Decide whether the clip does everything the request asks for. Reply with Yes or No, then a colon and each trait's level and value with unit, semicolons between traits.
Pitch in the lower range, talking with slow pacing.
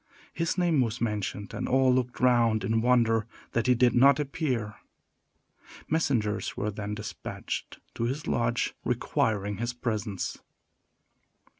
Yes: low, 120 Hz; slow, 130 wpm